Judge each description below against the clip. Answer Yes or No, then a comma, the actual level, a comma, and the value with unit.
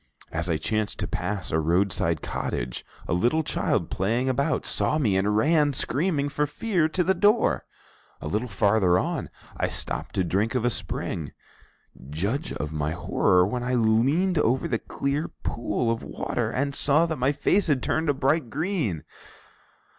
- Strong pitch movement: Yes, wide, 7.5 semitones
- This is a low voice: Yes, low, 120 Hz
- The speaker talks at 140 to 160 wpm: No, average, 170 wpm